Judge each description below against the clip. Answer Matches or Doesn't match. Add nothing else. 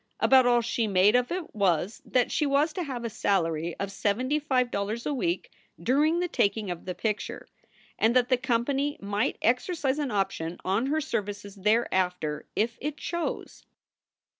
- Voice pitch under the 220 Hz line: Doesn't match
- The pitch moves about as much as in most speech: Doesn't match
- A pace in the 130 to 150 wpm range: Doesn't match